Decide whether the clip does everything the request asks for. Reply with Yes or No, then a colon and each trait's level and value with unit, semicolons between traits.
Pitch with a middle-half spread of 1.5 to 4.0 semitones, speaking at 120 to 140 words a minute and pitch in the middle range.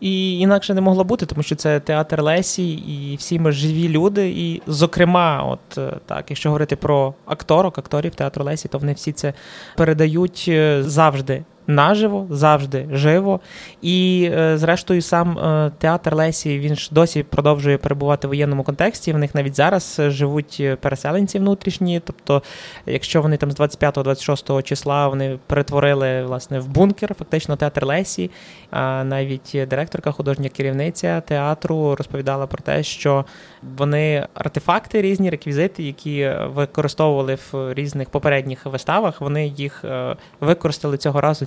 Yes: average, 3.3 semitones; average, 135 wpm; medium, 150 Hz